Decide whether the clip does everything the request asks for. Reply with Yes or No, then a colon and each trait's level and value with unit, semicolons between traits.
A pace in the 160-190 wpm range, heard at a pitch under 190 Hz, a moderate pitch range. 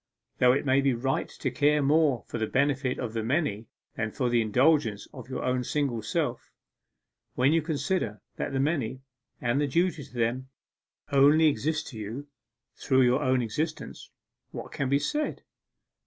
Yes: average, 170 wpm; low, 135 Hz; average, 3.3 semitones